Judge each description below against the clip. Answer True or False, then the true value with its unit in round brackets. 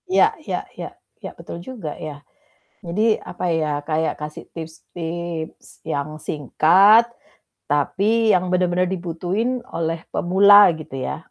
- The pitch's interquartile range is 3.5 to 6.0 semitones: True (4.2 semitones)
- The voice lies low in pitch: False (170 Hz)